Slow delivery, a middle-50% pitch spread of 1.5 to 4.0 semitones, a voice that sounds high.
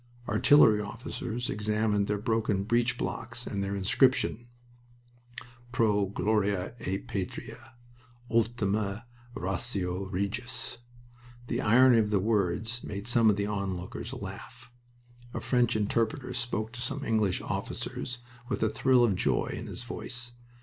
No: slow, 130 wpm; average, 3.1 semitones; low, 110 Hz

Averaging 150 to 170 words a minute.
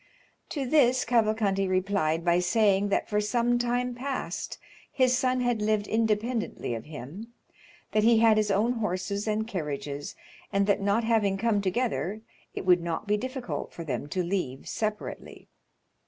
Yes: average, 155 wpm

